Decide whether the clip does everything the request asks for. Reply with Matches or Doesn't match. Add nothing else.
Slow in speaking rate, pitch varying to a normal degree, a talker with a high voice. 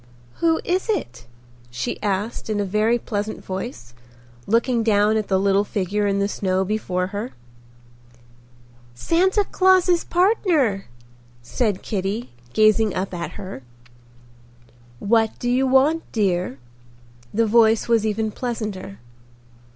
Matches